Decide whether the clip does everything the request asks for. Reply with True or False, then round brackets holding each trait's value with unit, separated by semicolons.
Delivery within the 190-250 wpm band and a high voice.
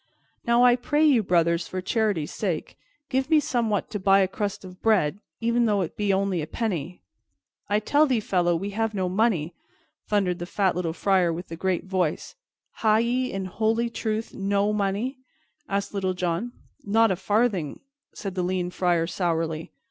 False (180 wpm; 195 Hz)